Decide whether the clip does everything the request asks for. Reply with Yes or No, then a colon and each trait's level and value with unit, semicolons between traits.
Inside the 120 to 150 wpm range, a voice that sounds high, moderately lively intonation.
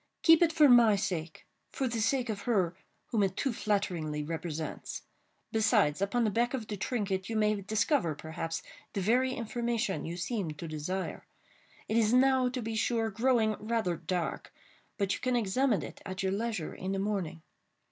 No: average, 170 wpm; high, 210 Hz; average, 4.5 semitones